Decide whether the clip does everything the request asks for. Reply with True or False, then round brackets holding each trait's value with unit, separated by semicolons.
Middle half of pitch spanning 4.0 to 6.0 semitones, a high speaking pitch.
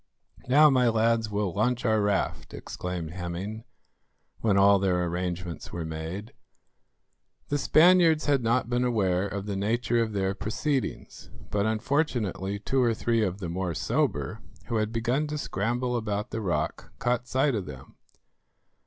False (4.4 semitones; 110 Hz)